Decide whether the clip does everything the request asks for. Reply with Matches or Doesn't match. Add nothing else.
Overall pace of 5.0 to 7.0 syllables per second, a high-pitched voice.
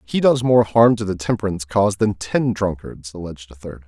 Doesn't match